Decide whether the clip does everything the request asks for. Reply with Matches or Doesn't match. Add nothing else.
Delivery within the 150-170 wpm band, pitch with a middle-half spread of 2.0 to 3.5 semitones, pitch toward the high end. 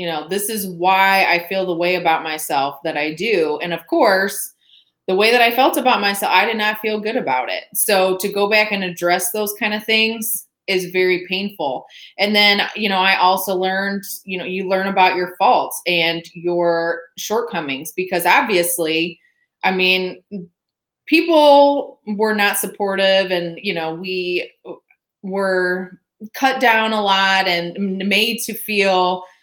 Matches